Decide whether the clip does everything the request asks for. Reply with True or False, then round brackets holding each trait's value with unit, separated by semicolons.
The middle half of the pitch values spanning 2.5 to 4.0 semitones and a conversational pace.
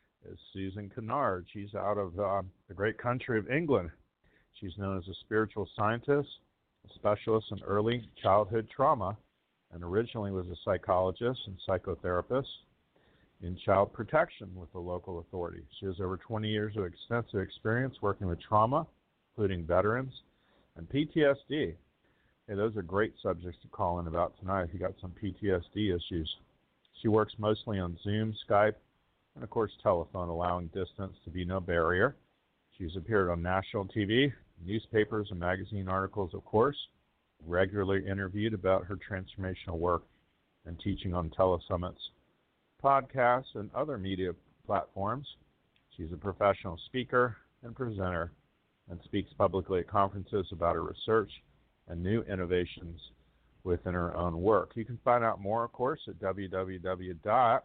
True (3.4 semitones; 145 wpm)